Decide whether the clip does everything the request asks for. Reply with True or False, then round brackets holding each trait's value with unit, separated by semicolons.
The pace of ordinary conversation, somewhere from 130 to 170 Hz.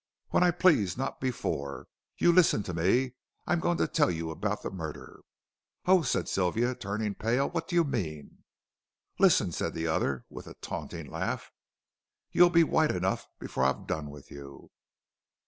False (170 wpm; 105 Hz)